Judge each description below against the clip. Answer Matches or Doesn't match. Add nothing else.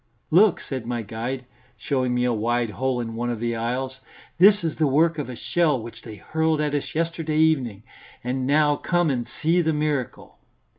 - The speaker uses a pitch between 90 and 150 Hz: Matches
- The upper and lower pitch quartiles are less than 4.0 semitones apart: Doesn't match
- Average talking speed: Matches